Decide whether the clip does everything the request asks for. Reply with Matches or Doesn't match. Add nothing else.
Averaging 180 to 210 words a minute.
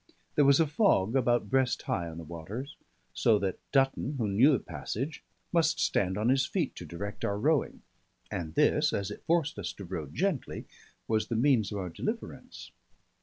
Matches